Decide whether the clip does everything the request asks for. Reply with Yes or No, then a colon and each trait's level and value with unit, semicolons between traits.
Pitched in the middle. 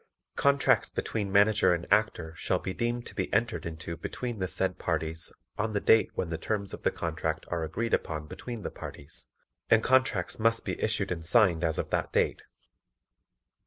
No: very low, 95 Hz